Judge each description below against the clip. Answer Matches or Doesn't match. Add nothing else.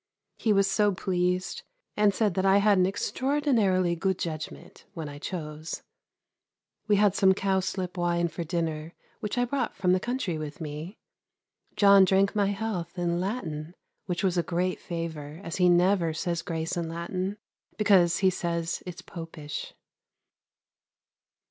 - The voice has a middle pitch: Matches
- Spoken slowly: Doesn't match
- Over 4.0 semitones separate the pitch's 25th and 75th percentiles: Doesn't match